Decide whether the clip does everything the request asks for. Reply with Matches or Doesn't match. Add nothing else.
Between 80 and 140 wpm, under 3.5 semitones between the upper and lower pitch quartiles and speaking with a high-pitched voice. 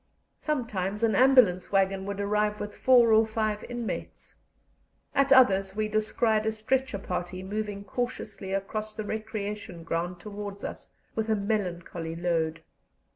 Matches